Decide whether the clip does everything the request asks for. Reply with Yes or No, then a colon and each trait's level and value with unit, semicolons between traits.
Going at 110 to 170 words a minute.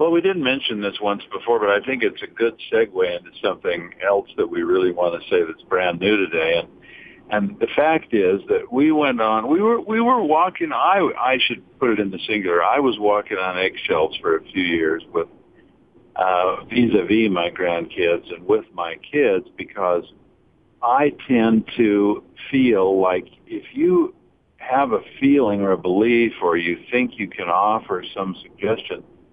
No: average, 185 wpm